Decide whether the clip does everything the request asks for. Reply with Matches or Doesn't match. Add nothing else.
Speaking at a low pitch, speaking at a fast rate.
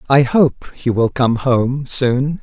Doesn't match